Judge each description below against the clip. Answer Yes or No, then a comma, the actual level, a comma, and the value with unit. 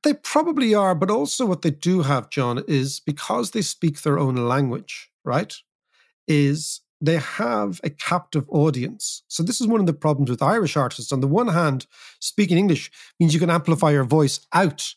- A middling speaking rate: Yes, average, 190 wpm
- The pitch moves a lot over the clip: No, average, 4.2 semitones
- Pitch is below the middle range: No, medium, 155 Hz